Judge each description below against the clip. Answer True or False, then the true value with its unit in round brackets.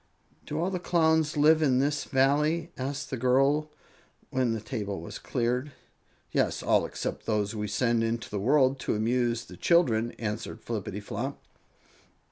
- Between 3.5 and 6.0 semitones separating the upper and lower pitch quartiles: True (4.7 semitones)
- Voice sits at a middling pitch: False (130 Hz)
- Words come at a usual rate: True (150 wpm)